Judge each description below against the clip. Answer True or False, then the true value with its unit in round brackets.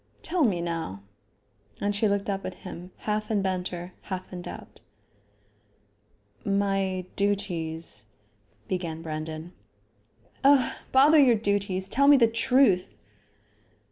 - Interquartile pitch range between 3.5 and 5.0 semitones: True (3.8 semitones)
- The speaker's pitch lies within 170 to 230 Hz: True (190 Hz)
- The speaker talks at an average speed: False (120 wpm)